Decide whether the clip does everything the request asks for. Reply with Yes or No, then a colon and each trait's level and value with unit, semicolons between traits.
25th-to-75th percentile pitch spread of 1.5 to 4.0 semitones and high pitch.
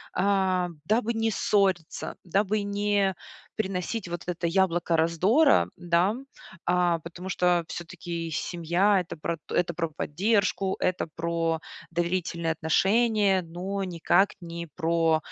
No: average, 2.8 semitones; medium, 180 Hz